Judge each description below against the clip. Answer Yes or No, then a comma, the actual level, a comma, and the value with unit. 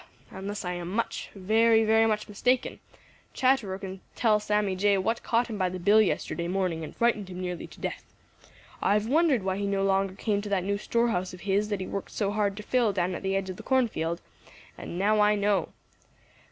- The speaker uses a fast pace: Yes, fast, 215 wpm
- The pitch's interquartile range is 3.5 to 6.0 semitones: No, narrow, 2.6 semitones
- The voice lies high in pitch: Yes, high, 200 Hz